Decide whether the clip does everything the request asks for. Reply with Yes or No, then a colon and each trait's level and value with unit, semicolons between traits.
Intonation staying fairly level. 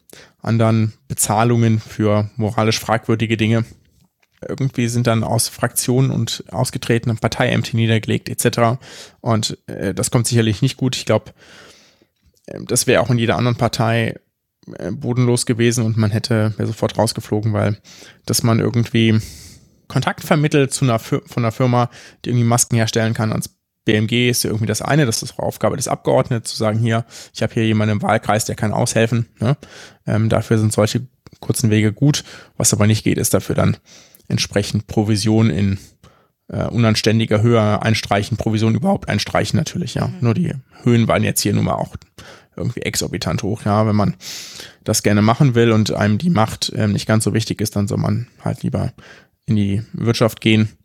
Yes: narrow, 2.0 semitones